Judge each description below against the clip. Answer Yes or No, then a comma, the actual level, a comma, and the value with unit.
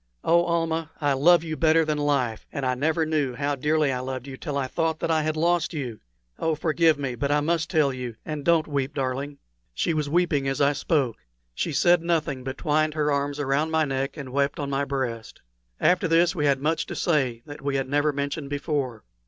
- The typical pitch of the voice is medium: Yes, medium, 145 Hz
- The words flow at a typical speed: No, fast, 220 wpm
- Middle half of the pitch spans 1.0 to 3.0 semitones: Yes, average, 2.7 semitones